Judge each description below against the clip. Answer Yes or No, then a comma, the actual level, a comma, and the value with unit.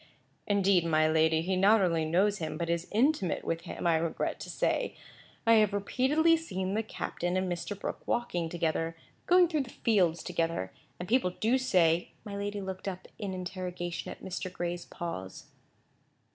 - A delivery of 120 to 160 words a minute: No, average, 175 wpm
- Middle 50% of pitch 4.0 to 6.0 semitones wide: No, average, 3.5 semitones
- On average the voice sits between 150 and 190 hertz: Yes, medium, 185 Hz